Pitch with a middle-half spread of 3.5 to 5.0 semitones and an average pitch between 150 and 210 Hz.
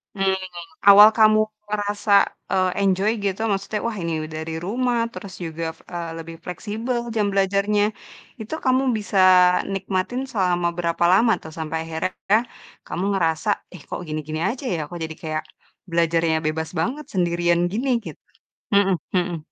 Yes: average, 3.8 semitones; medium, 185 Hz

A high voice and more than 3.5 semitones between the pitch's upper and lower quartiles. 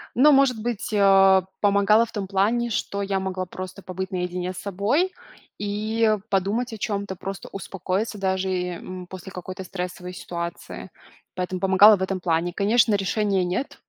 No: high, 195 Hz; narrow, 2.4 semitones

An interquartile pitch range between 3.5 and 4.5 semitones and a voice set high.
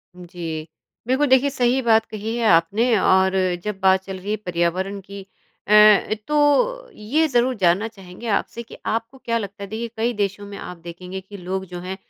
Yes: average, 4.0 semitones; high, 205 Hz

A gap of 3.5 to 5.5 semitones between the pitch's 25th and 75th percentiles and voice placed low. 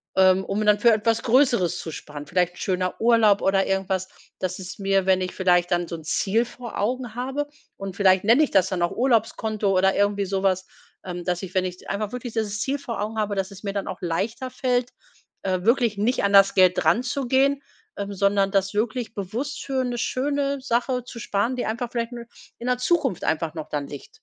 No: average, 4.3 semitones; high, 205 Hz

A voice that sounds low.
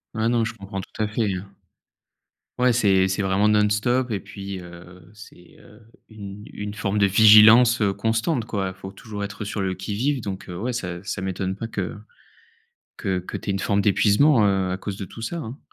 Yes: low, 100 Hz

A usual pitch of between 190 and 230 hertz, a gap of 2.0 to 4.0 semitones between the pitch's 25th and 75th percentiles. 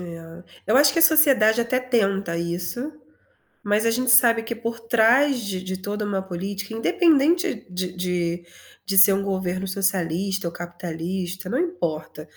No: high, 200 Hz; average, 4.9 semitones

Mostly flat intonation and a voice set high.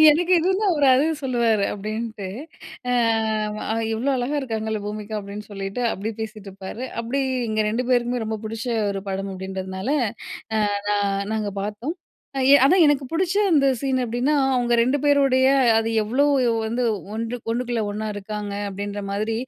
No: average, 3.8 semitones; high, 225 Hz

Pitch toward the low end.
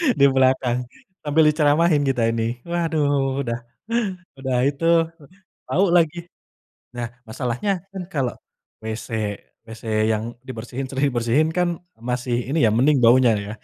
Yes: low, 130 Hz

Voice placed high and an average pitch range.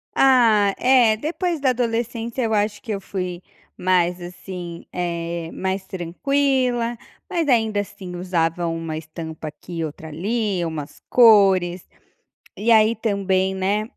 Yes: high, 195 Hz; average, 4.9 semitones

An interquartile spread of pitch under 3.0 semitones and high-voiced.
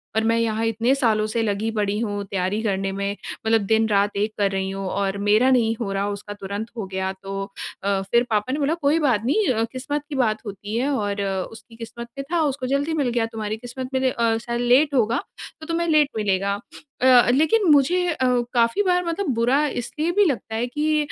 No: average, 5.0 semitones; high, 230 Hz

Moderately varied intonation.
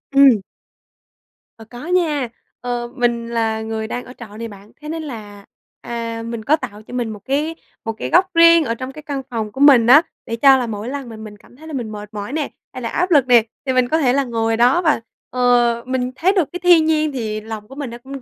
Yes: average, 4.1 semitones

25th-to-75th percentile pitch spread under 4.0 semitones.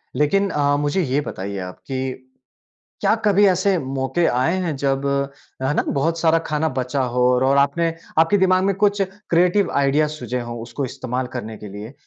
No: average, 5.1 semitones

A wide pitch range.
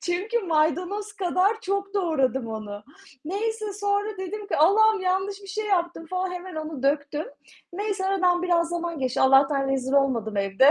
Yes: wide, 5.9 semitones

